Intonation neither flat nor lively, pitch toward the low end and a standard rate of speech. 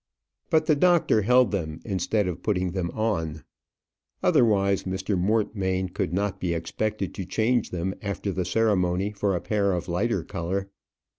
Yes: average, 3.0 semitones; low, 100 Hz; average, 155 wpm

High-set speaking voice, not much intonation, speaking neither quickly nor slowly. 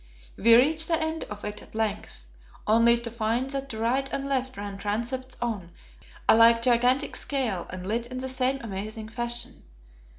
No: high, 235 Hz; average, 3.2 semitones; average, 175 wpm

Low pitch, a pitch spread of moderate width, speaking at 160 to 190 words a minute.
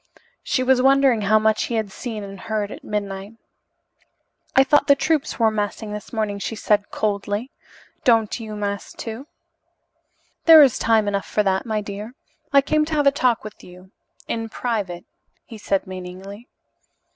No: high, 215 Hz; average, 3.5 semitones; average, 170 wpm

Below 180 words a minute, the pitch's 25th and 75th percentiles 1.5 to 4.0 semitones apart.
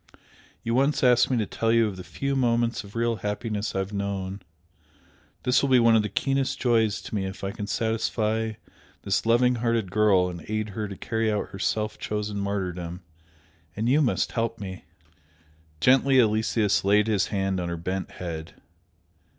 No: average, 185 wpm; average, 3.0 semitones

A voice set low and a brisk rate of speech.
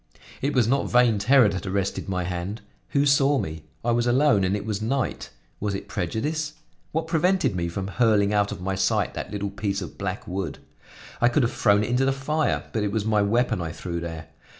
Yes: low, 105 Hz; fast, 220 wpm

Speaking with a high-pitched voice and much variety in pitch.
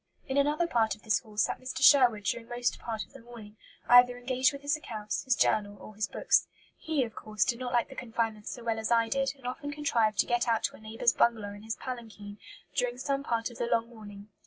No: high, 235 Hz; average, 2.8 semitones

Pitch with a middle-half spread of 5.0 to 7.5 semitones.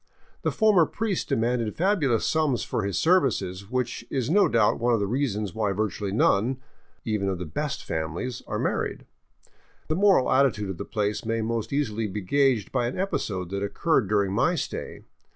Yes: wide, 5.6 semitones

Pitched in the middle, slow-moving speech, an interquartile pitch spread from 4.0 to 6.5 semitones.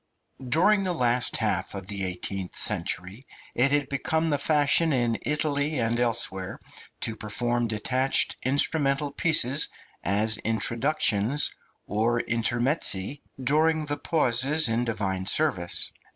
No: low, 120 Hz; slow, 120 wpm; average, 5.1 semitones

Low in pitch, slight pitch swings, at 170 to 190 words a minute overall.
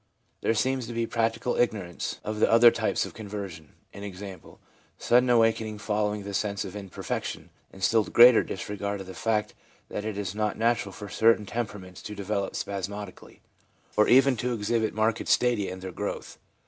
Yes: low, 105 Hz; narrow, 2.3 semitones; average, 175 wpm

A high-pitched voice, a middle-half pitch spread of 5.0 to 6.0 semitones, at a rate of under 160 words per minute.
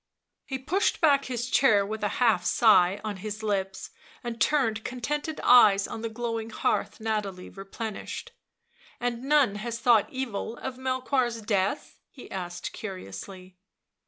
No: high, 225 Hz; average, 4.1 semitones; average, 150 wpm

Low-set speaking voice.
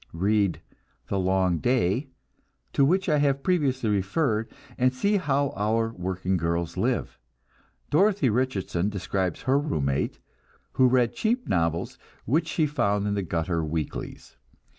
Yes: low, 110 Hz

